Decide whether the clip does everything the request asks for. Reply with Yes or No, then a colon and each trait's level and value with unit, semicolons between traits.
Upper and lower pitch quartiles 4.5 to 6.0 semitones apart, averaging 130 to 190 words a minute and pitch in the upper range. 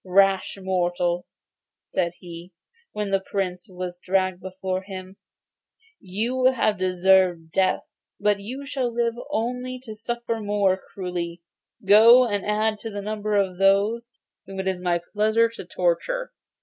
No: average, 3.3 semitones; average, 140 wpm; high, 195 Hz